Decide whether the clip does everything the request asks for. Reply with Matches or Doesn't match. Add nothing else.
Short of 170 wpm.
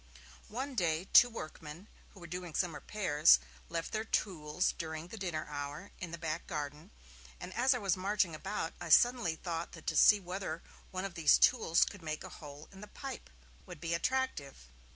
Doesn't match